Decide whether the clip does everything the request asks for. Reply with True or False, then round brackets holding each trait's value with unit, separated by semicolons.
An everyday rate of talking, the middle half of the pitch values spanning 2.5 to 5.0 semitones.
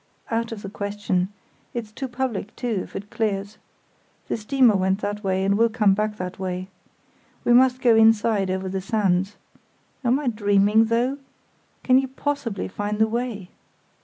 True (165 wpm; 3.2 semitones)